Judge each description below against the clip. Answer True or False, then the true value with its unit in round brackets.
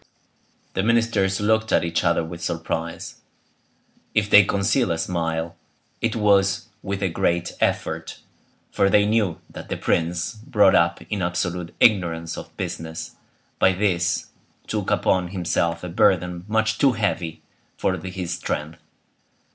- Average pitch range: True (3.5 semitones)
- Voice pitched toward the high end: False (90 Hz)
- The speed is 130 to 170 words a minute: True (140 wpm)